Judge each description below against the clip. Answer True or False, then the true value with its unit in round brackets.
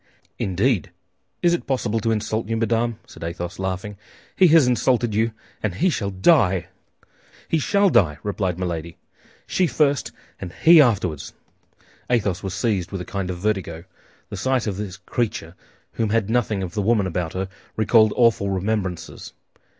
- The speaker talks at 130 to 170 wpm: True (160 wpm)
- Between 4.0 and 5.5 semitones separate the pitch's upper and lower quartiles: True (4.3 semitones)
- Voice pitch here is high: False (105 Hz)